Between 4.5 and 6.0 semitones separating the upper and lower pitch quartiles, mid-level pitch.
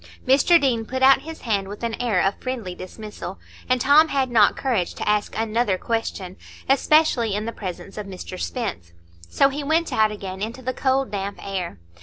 No: average, 5.0 semitones; high, 225 Hz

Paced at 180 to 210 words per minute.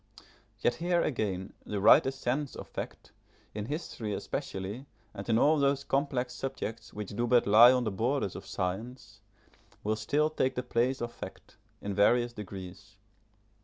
No: average, 160 wpm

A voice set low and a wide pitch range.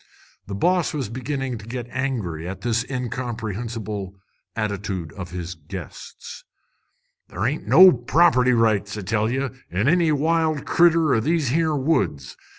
Yes: low, 120 Hz; wide, 6.2 semitones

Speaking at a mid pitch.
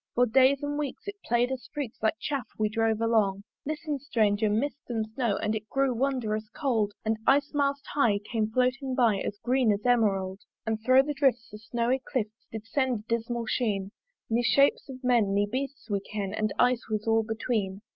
No: high, 230 Hz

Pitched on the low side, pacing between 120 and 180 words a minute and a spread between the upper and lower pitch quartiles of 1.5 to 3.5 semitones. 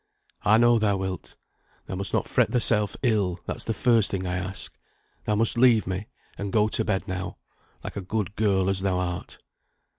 No: low, 100 Hz; average, 190 wpm; average, 2.7 semitones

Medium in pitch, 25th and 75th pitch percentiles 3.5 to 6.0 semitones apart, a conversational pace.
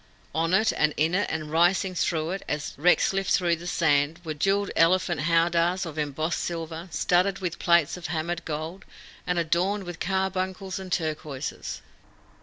No: medium, 170 Hz; average, 2.8 semitones; average, 165 wpm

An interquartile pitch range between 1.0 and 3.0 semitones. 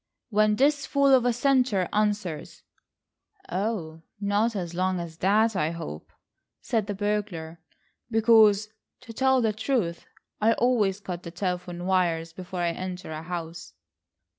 No: average, 4.3 semitones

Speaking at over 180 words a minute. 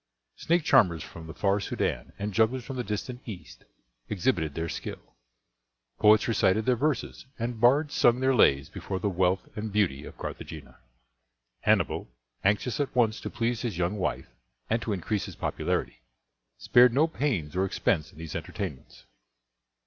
No: average, 160 wpm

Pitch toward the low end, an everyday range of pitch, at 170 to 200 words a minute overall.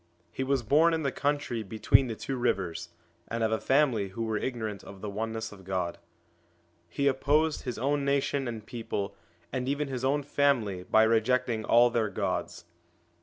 Yes: low, 120 Hz; average, 4.1 semitones; average, 180 wpm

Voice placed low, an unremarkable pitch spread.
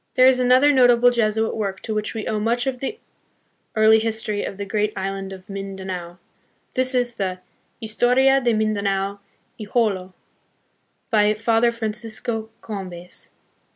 No: high, 220 Hz; average, 3.4 semitones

